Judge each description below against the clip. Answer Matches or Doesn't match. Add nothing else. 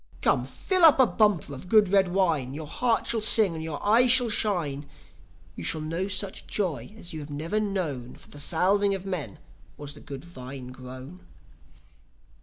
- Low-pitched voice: Doesn't match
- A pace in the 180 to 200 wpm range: Matches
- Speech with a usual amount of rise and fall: Doesn't match